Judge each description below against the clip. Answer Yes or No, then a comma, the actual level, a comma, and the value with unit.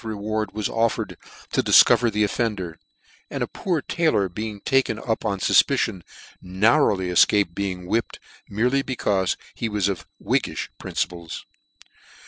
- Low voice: Yes, low, 105 Hz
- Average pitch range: Yes, average, 3.4 semitones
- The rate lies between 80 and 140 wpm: Yes, slow, 135 wpm